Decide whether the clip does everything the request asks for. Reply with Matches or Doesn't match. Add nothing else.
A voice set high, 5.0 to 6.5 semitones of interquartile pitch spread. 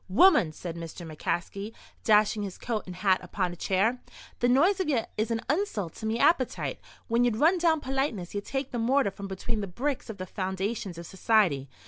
Matches